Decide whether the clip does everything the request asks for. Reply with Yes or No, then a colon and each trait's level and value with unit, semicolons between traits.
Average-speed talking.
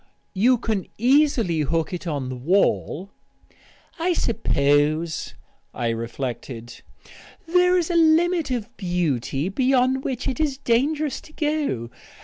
No: slow, 130 wpm